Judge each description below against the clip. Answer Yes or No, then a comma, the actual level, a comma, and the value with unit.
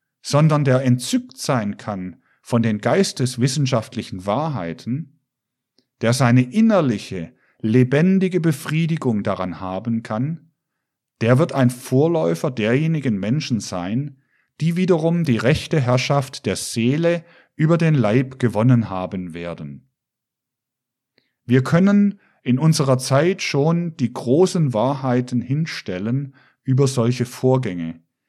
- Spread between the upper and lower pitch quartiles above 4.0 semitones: Yes, average, 4.7 semitones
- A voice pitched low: Yes, low, 130 Hz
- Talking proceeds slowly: Yes, slow, 105 wpm